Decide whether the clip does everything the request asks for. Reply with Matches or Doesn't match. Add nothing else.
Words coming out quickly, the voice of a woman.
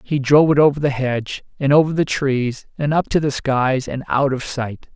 Doesn't match